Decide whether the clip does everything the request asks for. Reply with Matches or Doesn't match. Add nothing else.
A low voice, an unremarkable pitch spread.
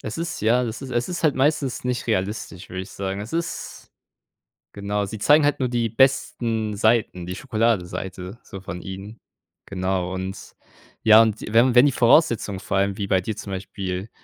Matches